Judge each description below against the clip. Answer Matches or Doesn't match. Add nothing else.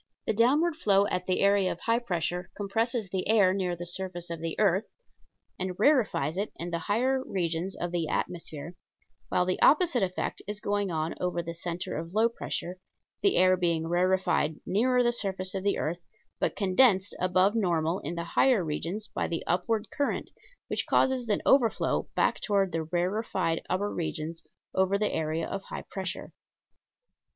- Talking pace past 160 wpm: Matches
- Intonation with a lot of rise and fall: Doesn't match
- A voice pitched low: Doesn't match